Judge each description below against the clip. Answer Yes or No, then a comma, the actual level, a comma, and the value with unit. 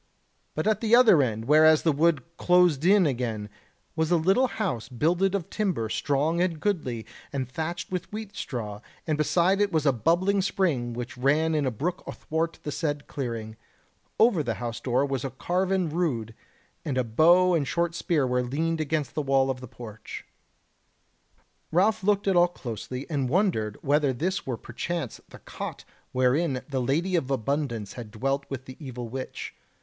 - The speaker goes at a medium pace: Yes, average, 175 wpm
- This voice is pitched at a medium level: Yes, medium, 150 Hz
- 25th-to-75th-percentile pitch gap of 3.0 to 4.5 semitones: No, wide, 5.6 semitones